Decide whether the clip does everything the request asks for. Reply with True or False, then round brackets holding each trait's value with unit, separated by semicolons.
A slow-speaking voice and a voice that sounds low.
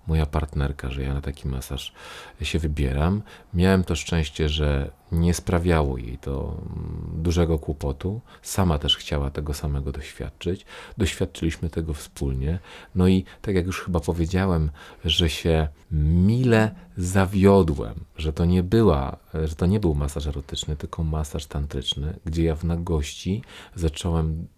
False (140 wpm; 80 Hz)